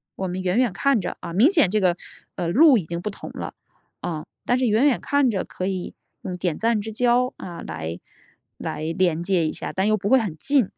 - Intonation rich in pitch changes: Yes, wide, 5.7 semitones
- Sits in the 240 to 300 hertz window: No, high, 195 Hz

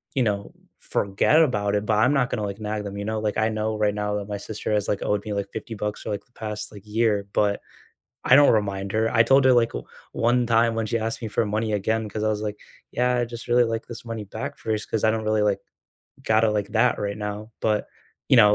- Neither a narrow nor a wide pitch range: No, narrow, 1.7 semitones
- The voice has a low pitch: Yes, low, 110 Hz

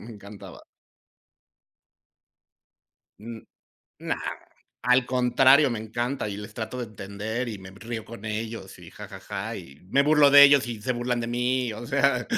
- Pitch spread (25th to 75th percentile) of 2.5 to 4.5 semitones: Yes, average, 2.9 semitones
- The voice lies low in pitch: Yes, low, 120 Hz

